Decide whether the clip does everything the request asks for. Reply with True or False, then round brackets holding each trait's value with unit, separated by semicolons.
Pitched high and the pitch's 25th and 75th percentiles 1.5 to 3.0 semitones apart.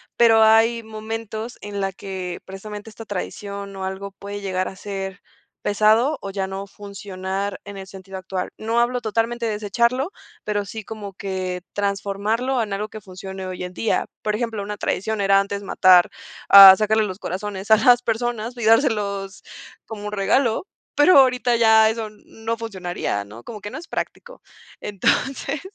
True (205 Hz; 2.6 semitones)